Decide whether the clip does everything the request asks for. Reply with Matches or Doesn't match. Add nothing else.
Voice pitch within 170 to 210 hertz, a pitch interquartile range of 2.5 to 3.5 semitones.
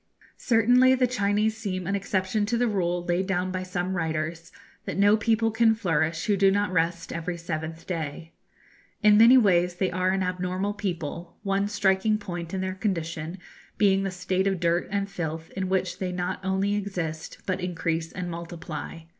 Matches